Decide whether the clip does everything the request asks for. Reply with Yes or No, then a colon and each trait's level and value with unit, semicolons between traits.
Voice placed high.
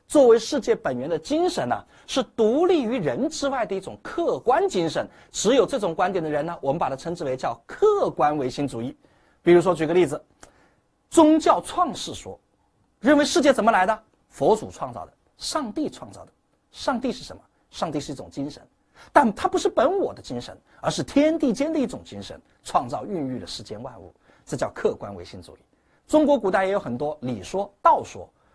Yes: very high, 260 Hz